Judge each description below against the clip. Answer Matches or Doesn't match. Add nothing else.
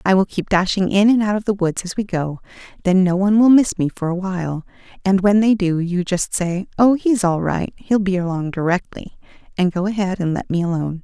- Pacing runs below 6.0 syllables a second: Matches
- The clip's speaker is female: Matches